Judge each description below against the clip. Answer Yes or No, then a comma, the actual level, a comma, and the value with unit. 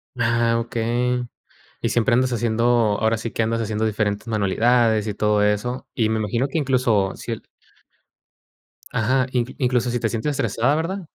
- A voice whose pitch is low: Yes, low, 115 Hz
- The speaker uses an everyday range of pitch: No, narrow, 2.2 semitones